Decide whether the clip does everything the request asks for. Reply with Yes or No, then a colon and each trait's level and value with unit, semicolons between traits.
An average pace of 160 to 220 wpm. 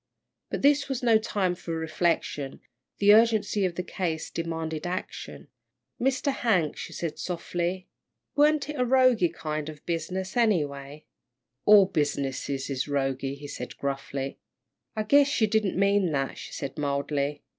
No: average, 150 wpm